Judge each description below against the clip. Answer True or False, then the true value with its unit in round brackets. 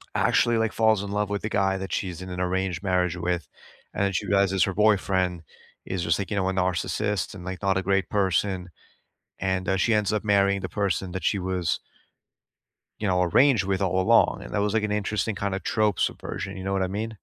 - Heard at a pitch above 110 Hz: False (95 Hz)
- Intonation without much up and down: True (1.8 semitones)